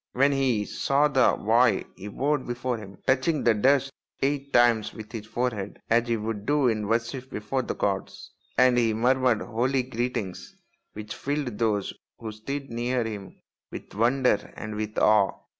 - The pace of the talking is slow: No, average, 165 wpm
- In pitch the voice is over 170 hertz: No, low, 120 Hz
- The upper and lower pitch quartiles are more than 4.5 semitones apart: No, average, 3.4 semitones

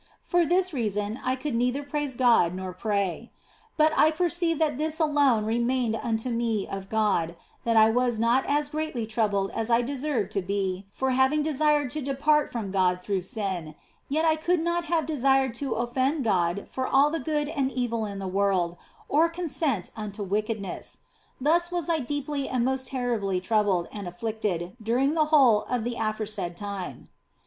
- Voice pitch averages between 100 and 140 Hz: No, high, 240 Hz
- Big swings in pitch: Yes, wide, 6.2 semitones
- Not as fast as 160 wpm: No, average, 175 wpm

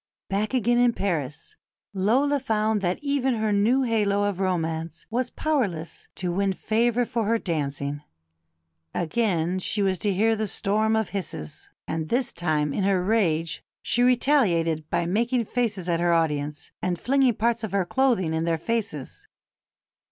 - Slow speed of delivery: No, average, 160 wpm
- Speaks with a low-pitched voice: No, high, 200 Hz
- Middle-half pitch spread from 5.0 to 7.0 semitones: Yes, wide, 5.5 semitones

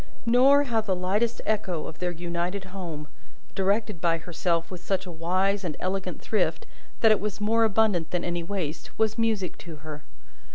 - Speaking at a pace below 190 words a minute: Yes, average, 175 wpm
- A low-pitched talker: No, medium, 185 Hz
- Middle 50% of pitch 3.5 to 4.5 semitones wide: Yes, average, 3.8 semitones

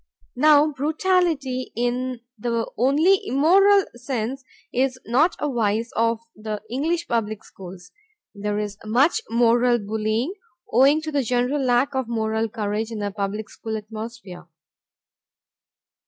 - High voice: Yes, high, 240 Hz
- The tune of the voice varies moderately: Yes, average, 4.3 semitones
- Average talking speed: No, slow, 125 wpm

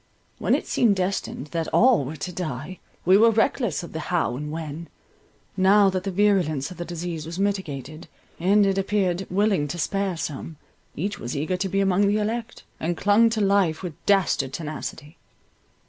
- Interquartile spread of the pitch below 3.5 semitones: No, average, 4.1 semitones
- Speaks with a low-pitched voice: No, medium, 185 Hz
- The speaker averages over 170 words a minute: Yes, average, 180 wpm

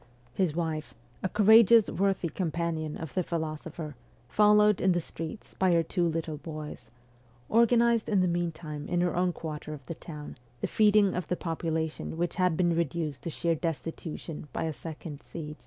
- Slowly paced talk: No, average, 175 wpm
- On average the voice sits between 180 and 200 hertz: No, medium, 170 Hz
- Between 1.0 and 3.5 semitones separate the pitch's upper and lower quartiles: Yes, average, 2.8 semitones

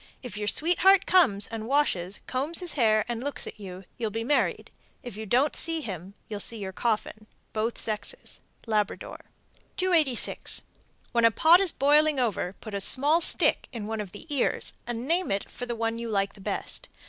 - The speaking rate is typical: Yes, average, 185 wpm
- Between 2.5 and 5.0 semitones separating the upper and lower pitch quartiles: No, wide, 5.6 semitones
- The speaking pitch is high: Yes, high, 230 Hz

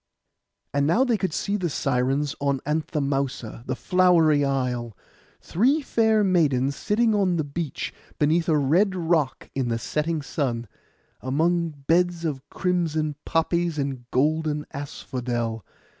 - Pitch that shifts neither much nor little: Yes, average, 4.3 semitones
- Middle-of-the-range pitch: Yes, medium, 150 Hz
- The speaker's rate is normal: No, slow, 130 wpm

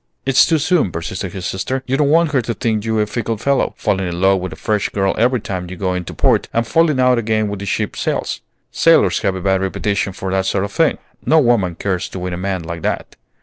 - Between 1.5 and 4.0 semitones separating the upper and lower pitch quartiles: No, average, 4.7 semitones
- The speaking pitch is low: Yes, low, 100 Hz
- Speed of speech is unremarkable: No, fast, 250 wpm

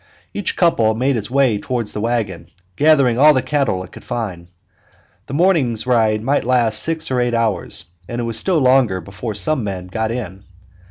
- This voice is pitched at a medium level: No, low, 120 Hz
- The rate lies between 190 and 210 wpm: Yes, average, 200 wpm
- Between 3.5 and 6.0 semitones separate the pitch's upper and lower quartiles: Yes, average, 4.0 semitones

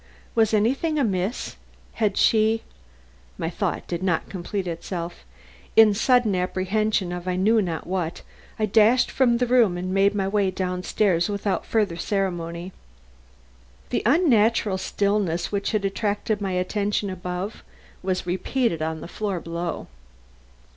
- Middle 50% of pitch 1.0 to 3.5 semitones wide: Yes, average, 3.1 semitones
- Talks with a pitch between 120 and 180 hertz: No, high, 195 Hz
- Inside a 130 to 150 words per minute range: Yes, average, 140 wpm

